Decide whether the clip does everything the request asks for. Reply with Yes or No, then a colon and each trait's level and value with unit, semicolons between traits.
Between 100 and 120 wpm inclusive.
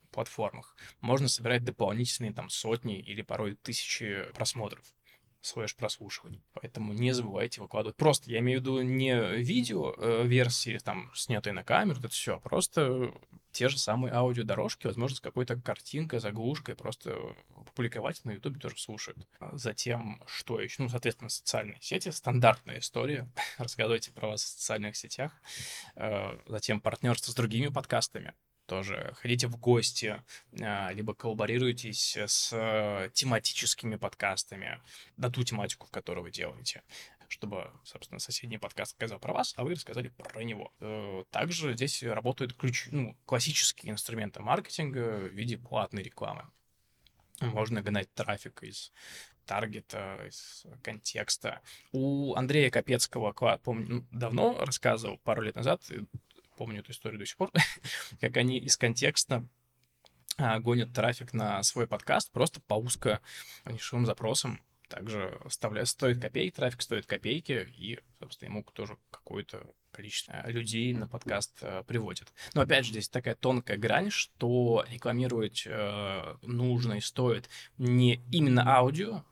No: average, 135 wpm